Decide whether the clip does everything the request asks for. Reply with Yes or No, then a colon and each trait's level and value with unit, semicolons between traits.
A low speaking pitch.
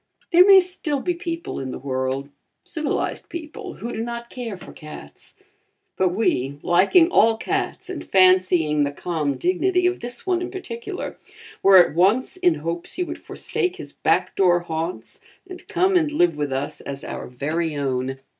No: high, 195 Hz